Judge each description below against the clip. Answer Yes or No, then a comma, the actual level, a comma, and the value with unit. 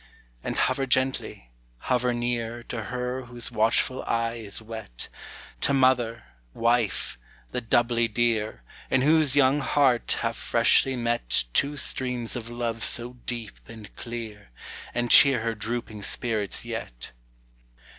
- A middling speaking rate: No, slow, 130 wpm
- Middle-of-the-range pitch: No, low, 120 Hz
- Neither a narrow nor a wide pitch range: No, narrow, 2.1 semitones